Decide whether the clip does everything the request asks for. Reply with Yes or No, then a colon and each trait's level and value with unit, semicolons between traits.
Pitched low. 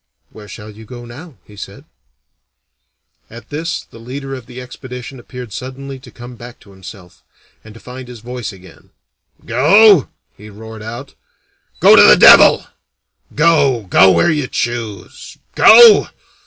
Yes: low, 125 Hz